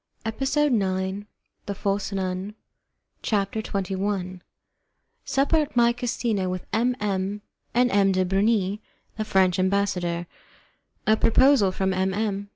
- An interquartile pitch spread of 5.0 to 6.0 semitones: No, average, 2.8 semitones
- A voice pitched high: Yes, high, 200 Hz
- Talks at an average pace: No, slow, 125 wpm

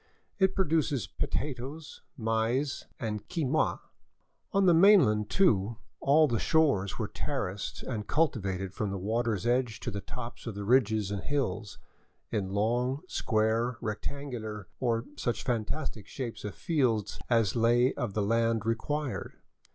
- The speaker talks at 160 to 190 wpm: No, average, 145 wpm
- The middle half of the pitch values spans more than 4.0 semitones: Yes, average, 4.6 semitones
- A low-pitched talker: Yes, low, 115 Hz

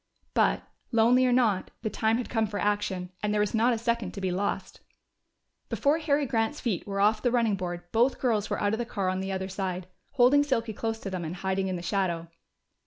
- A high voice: Yes, high, 210 Hz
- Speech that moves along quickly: Yes, fast, 230 wpm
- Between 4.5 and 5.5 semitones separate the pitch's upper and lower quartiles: No, average, 3.8 semitones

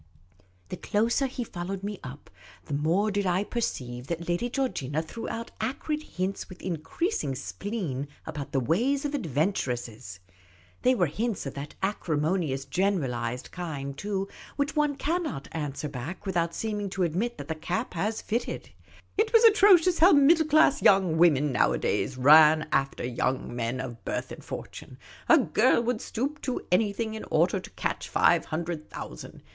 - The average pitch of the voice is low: No, medium, 180 Hz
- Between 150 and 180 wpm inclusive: Yes, average, 160 wpm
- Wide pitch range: Yes, wide, 8.4 semitones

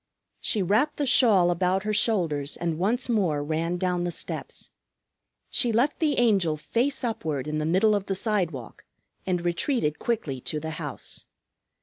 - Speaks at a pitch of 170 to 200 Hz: Yes, medium, 185 Hz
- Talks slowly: No, average, 160 wpm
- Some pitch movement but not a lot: No, wide, 6.1 semitones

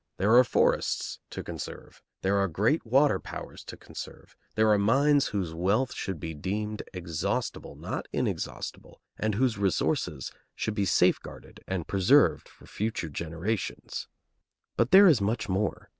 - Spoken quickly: No, average, 145 wpm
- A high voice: No, low, 105 Hz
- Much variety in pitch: No, average, 3.5 semitones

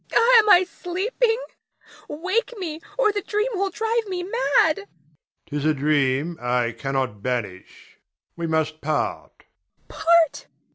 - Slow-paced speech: Yes, slow, 130 wpm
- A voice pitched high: Yes, very high, 310 Hz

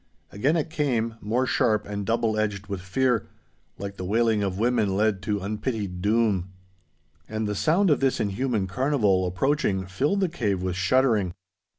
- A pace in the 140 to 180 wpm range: Yes, average, 165 wpm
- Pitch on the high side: No, low, 110 Hz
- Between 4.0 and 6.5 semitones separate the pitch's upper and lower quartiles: Yes, average, 4.5 semitones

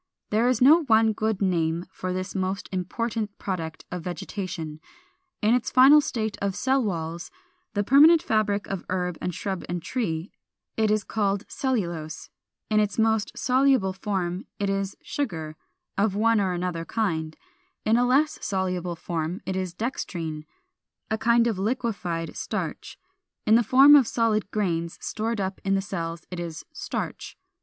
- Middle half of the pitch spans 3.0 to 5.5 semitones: Yes, average, 4.2 semitones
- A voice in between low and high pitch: No, high, 200 Hz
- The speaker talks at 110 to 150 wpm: No, average, 160 wpm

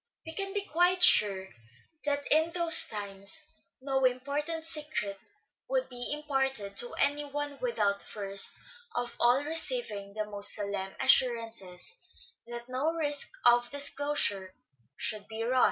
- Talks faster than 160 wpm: No, slow, 135 wpm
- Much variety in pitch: Yes, wide, 6.3 semitones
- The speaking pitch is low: No, very high, 255 Hz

